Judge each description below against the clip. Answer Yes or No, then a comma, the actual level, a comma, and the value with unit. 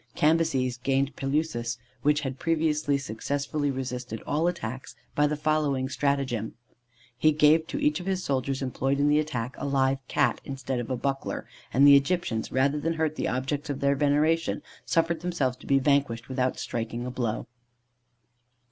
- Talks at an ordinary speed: Yes, average, 165 wpm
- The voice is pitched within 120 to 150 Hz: Yes, medium, 140 Hz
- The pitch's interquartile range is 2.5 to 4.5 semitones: Yes, average, 2.9 semitones